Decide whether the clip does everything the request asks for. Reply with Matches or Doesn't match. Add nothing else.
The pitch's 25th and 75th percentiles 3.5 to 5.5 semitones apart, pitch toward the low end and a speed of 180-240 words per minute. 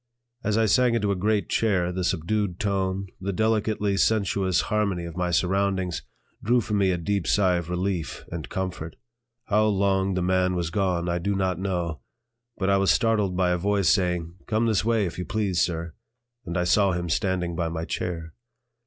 Doesn't match